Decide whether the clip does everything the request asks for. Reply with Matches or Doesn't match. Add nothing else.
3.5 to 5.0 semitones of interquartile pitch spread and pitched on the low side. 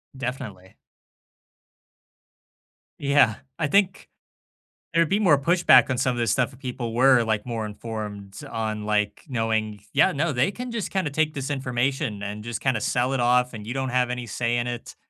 Matches